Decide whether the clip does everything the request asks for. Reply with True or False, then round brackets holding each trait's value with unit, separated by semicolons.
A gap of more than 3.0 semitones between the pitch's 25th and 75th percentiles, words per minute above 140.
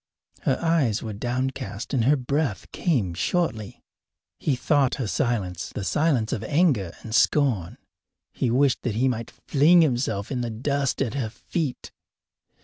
True (4.6 semitones; 150 wpm)